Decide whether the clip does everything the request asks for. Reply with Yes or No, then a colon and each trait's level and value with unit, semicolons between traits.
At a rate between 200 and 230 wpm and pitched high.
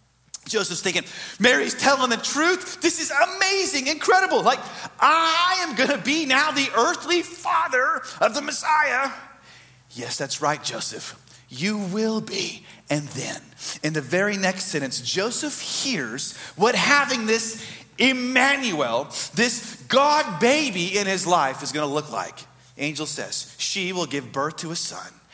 No: average, 150 wpm; high, 225 Hz